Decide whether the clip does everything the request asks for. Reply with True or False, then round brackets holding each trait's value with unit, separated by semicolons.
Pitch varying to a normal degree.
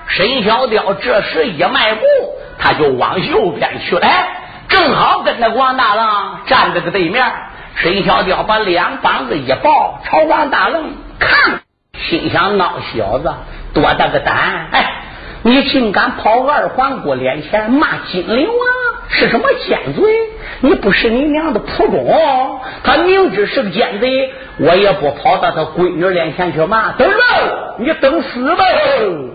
False (7.4 semitones)